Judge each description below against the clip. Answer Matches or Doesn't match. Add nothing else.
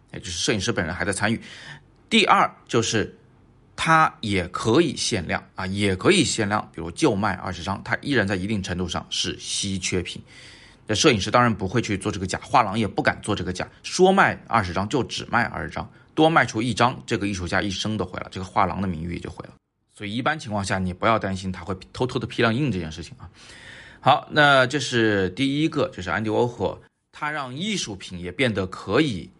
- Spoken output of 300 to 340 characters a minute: Matches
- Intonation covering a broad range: Doesn't match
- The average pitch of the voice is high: Doesn't match